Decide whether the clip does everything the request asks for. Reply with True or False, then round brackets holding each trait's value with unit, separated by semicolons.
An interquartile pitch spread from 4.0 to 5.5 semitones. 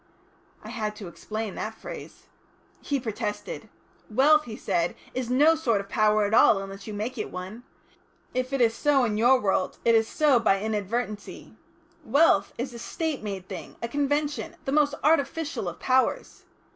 True (4.7 semitones)